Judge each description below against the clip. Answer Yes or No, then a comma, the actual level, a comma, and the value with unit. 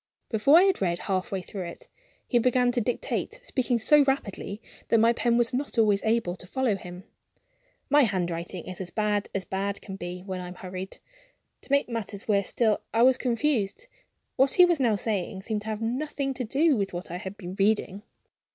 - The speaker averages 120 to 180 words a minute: No, fast, 205 wpm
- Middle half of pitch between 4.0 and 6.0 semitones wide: Yes, average, 4.7 semitones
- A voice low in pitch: No, high, 215 Hz